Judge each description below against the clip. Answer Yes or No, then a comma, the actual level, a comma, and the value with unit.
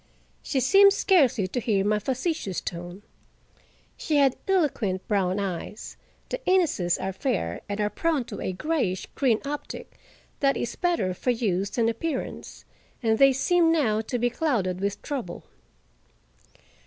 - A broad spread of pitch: Yes, wide, 7.1 semitones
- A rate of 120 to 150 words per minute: Yes, average, 140 wpm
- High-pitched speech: Yes, high, 235 Hz